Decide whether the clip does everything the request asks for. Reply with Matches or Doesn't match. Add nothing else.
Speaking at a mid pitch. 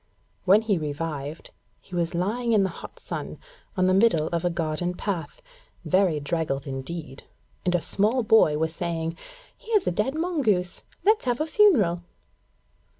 Matches